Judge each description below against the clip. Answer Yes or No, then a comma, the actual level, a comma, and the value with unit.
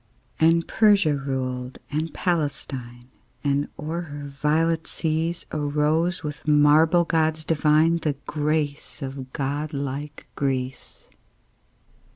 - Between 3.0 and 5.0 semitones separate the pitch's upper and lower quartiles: No, narrow, 2.4 semitones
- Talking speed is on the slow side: Yes, slow, 105 wpm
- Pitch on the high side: No, medium, 150 Hz